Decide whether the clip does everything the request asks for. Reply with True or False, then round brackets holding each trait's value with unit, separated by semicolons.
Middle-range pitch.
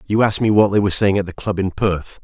False (100 Hz)